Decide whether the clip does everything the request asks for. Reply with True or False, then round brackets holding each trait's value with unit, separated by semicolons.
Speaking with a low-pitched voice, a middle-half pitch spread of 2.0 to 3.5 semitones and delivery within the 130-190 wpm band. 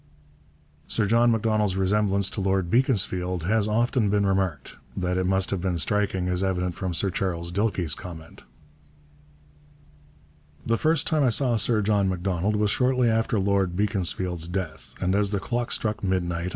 True (95 Hz; 2.9 semitones; 160 wpm)